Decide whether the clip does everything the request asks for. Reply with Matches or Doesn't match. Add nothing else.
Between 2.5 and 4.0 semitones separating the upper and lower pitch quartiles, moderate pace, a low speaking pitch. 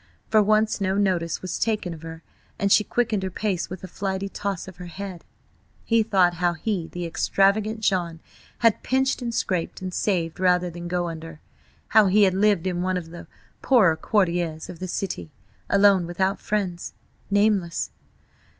Doesn't match